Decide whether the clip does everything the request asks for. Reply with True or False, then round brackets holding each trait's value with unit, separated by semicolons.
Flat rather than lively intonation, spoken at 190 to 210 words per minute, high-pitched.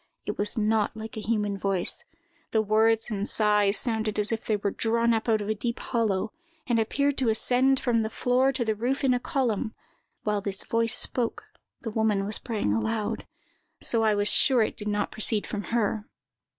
True (1.9 semitones; 200 wpm; 220 Hz)